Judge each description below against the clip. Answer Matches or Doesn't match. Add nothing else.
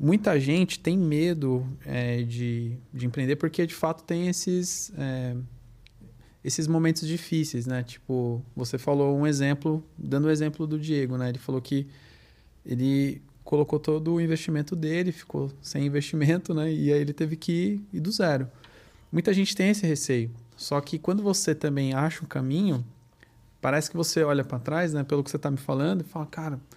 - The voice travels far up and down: Doesn't match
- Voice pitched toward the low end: Doesn't match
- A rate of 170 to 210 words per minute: Matches